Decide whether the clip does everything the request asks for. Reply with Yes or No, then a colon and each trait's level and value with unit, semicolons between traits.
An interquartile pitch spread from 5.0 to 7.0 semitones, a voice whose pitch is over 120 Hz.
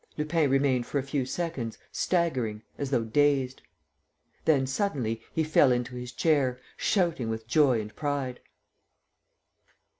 No: average, 3.6 semitones; low, 135 Hz